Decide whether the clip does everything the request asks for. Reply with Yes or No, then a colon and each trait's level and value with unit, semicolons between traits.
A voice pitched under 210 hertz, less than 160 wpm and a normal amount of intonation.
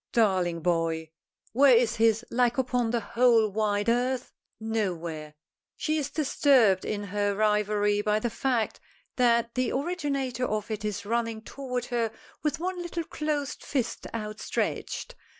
No: high, 230 Hz; average, 140 wpm; average, 3.6 semitones